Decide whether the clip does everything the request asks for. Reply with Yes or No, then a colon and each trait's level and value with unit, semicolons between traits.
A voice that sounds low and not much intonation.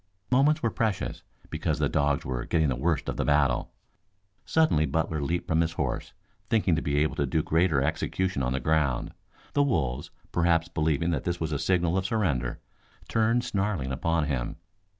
No: very low, 80 Hz; average, 4.7 semitones